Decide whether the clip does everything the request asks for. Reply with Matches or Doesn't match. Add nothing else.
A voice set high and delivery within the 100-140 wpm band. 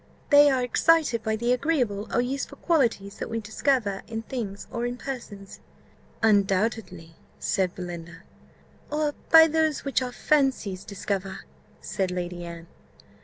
Matches